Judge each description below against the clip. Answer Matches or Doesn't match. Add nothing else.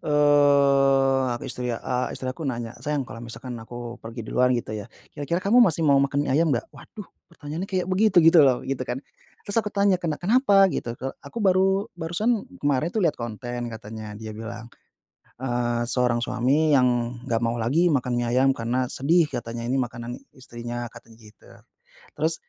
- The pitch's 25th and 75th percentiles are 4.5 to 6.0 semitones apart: Matches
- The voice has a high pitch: Doesn't match